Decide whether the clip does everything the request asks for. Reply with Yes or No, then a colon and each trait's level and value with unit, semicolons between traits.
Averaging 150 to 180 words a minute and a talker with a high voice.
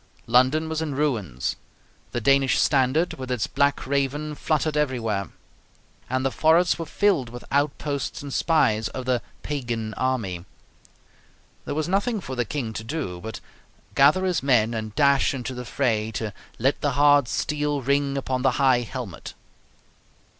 No: average, 155 wpm; low, 135 Hz